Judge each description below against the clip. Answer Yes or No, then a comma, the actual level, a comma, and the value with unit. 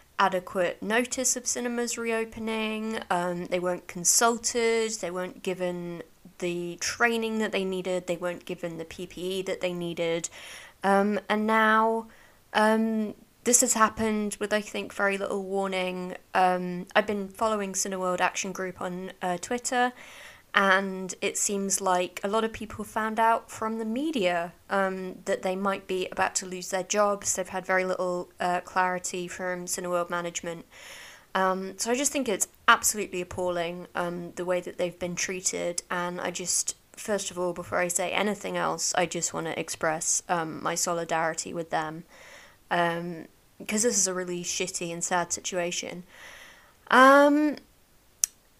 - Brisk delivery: No, average, 155 wpm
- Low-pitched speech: No, medium, 185 Hz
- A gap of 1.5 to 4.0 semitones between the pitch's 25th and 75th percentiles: Yes, average, 3.5 semitones